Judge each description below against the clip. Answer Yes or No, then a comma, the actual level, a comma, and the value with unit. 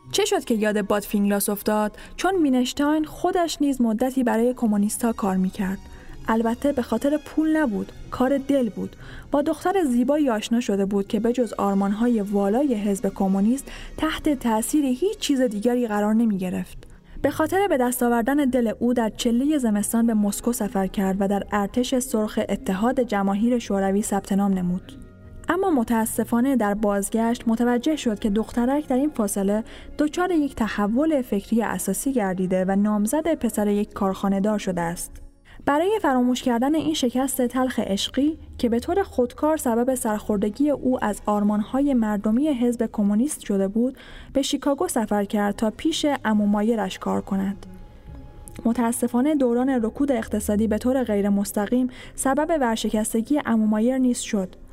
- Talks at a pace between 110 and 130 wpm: No, average, 145 wpm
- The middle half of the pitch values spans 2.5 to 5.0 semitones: Yes, average, 4.4 semitones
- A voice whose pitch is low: No, high, 230 Hz